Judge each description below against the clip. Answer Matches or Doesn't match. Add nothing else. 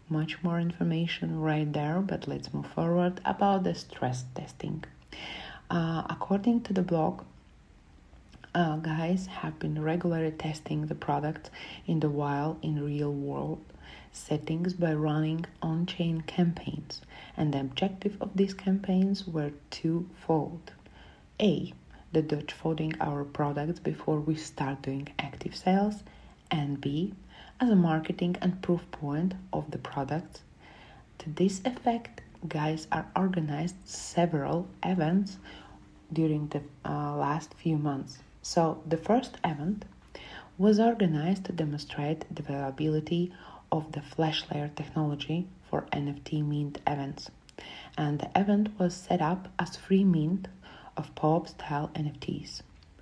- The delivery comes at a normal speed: Doesn't match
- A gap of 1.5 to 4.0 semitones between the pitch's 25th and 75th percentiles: Matches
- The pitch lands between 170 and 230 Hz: Doesn't match